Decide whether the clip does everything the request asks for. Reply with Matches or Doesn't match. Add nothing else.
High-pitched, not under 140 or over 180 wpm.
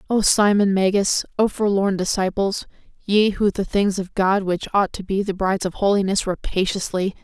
Matches